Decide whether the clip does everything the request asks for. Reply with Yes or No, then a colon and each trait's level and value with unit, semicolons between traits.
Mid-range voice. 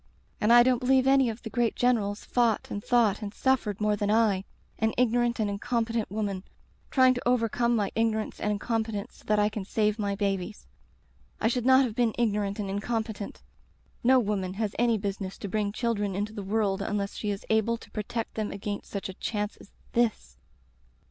No: high, 215 Hz